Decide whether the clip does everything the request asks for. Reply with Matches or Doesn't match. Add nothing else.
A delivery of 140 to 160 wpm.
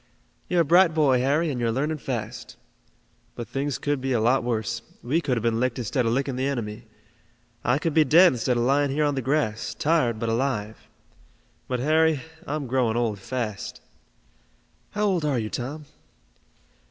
Doesn't match